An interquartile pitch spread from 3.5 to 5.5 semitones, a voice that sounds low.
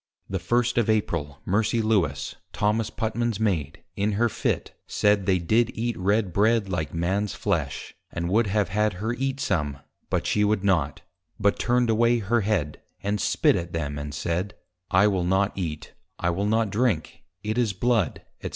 Yes: average, 4.0 semitones; low, 100 Hz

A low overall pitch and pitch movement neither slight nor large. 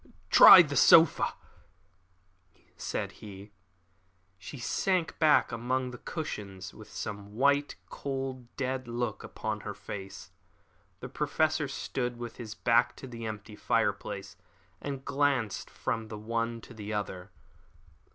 Yes: low, 120 Hz; average, 4.1 semitones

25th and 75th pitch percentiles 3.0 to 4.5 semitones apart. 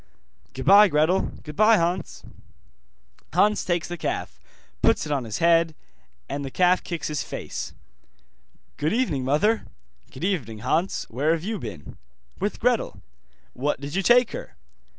No: average, 5.1 semitones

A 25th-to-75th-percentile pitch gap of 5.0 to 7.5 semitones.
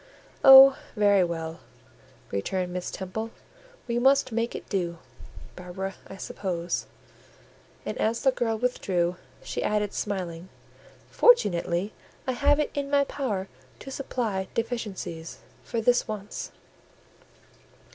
Yes: average, 5.3 semitones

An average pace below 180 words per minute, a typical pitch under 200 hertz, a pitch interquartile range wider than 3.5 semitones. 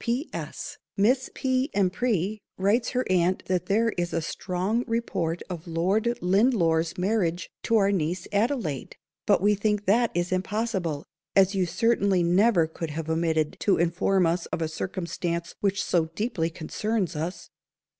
Yes: average, 155 wpm; medium, 185 Hz; average, 4.1 semitones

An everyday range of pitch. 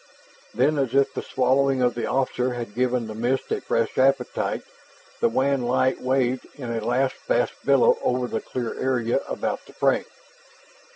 No: narrow, 2.0 semitones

